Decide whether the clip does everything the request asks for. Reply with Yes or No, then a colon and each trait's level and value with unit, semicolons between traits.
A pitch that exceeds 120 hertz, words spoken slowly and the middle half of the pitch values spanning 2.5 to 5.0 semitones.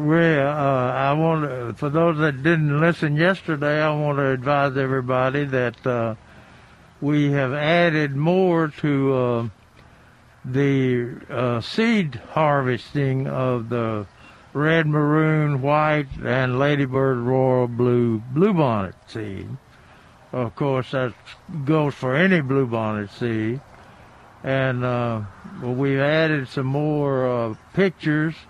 Yes: low, 135 Hz; slow, 115 wpm; average, 3.5 semitones